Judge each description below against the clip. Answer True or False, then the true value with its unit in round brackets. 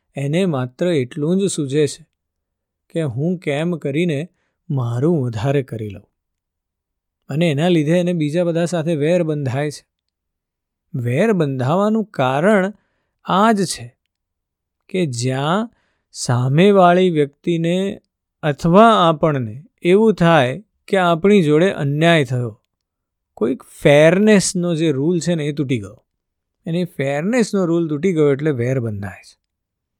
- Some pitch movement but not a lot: False (6.7 semitones)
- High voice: False (150 Hz)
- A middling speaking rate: True (120 wpm)